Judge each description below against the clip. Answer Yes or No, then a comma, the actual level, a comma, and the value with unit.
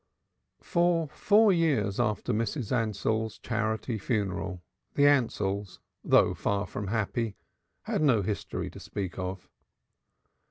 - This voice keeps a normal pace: No, slow, 115 wpm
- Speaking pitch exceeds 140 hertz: No, low, 110 Hz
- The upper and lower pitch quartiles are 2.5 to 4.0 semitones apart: No, average, 5.1 semitones